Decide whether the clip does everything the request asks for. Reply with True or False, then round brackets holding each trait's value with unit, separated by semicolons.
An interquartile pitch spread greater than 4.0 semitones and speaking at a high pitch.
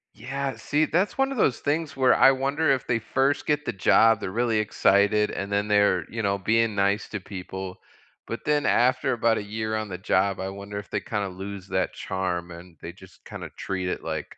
False (5.0 semitones; 105 Hz)